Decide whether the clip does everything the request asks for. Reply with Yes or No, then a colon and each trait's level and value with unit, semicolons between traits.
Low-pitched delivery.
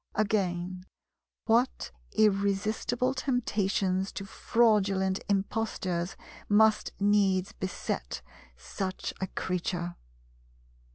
No: high, 195 Hz